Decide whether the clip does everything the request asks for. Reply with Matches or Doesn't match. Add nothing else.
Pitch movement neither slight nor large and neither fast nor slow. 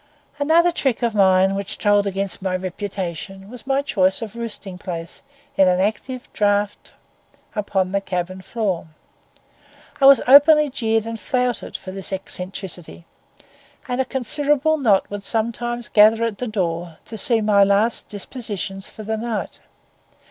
Matches